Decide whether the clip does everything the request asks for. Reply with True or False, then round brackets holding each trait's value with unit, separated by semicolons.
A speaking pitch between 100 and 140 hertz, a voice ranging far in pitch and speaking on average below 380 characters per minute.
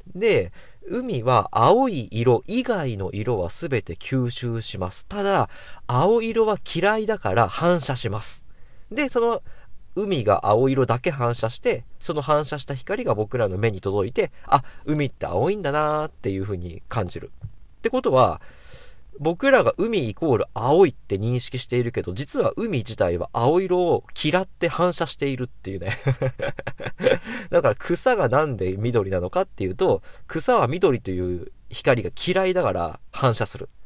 True (135 Hz; 8.4 semitones; 290 characters per minute)